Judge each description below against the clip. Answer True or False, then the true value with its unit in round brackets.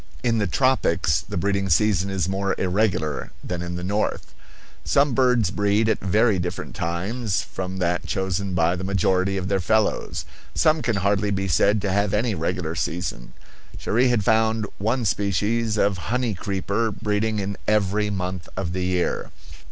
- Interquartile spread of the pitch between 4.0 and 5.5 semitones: False (3.0 semitones)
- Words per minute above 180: False (165 wpm)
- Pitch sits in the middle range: False (100 Hz)